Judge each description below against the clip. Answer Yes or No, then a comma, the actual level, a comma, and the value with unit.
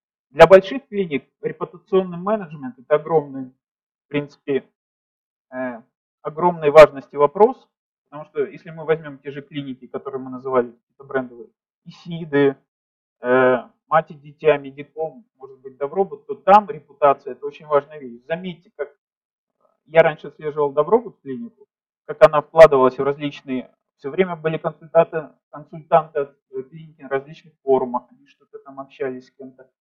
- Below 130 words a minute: No, average, 135 wpm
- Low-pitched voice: No, medium, 155 Hz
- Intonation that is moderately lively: No, wide, 6.3 semitones